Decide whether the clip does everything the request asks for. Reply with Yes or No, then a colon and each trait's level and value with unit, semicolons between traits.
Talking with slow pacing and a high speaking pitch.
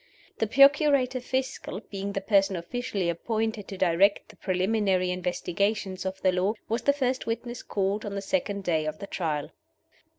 No: average, 165 wpm; high, 200 Hz